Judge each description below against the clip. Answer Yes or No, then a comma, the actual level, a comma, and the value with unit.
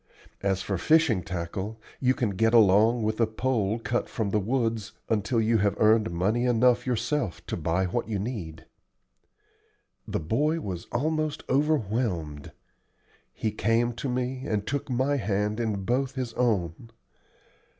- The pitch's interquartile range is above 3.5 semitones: Yes, average, 4.0 semitones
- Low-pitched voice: Yes, low, 110 Hz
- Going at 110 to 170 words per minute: Yes, average, 150 wpm